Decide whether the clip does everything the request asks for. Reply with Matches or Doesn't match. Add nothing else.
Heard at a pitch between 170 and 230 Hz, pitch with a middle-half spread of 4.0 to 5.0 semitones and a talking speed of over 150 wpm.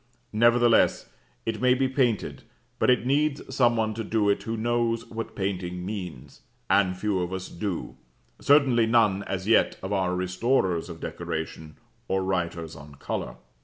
Doesn't match